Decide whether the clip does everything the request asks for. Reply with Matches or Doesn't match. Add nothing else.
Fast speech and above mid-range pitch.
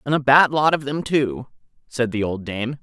Doesn't match